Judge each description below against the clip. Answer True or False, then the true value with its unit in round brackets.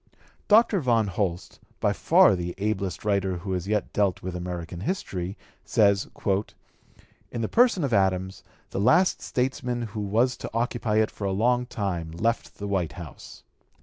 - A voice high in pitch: False (100 Hz)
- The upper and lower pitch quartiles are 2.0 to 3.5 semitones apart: False (4.2 semitones)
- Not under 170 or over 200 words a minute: False (160 wpm)